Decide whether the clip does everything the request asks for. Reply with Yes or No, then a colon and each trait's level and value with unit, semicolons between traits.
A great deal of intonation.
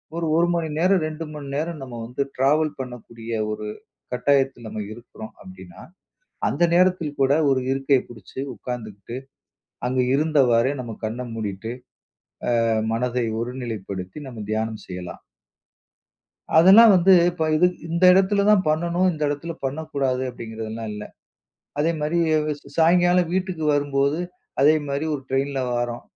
Yes: wide, 5.7 semitones